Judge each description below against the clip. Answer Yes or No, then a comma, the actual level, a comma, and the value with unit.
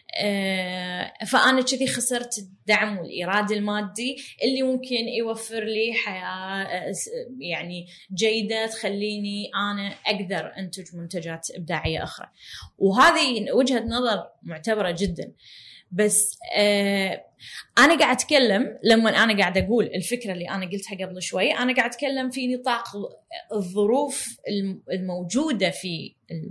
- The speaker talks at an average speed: Yes, average, 110 wpm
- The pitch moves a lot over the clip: No, average, 4.2 semitones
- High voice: Yes, high, 210 Hz